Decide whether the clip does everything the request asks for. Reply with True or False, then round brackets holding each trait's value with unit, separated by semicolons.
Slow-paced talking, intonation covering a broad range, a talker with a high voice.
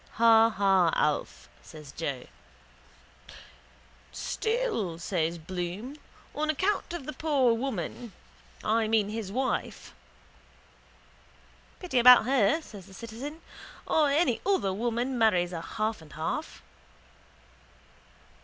True (105 wpm; 6.5 semitones; 225 Hz)